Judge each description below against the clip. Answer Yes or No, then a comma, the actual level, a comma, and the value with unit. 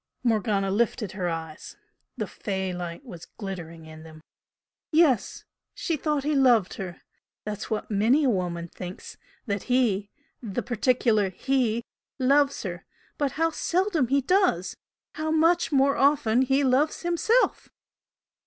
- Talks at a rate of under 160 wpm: Yes, slow, 135 wpm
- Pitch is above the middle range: Yes, high, 235 Hz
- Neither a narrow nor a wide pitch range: No, wide, 6.8 semitones